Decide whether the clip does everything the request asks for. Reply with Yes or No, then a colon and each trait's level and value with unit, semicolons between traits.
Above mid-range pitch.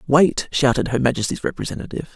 No: low, 135 Hz